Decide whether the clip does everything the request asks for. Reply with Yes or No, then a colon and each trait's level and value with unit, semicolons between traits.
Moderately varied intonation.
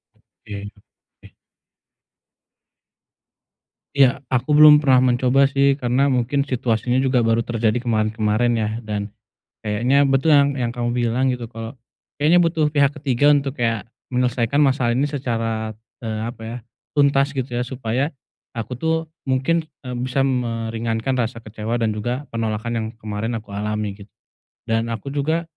Yes: average, 3.5 semitones